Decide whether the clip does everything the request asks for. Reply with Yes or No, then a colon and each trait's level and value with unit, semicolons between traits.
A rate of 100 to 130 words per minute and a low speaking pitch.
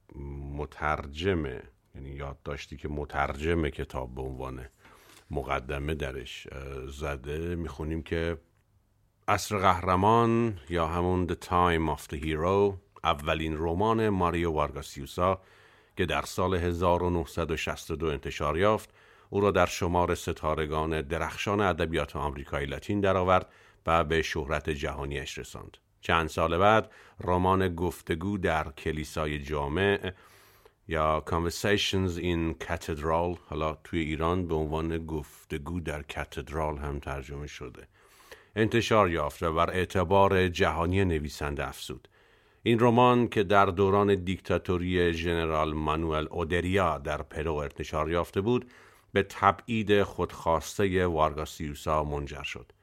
Yes: average, 110 wpm; very low, 85 Hz